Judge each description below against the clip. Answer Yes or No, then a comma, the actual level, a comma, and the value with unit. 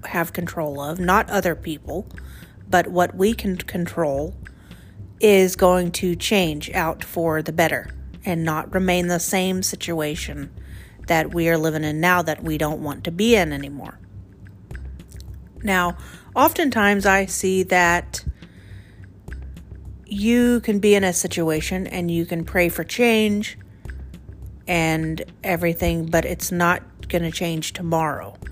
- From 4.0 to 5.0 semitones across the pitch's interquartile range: No, average, 3.4 semitones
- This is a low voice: No, medium, 170 Hz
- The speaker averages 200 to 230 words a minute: No, slow, 135 wpm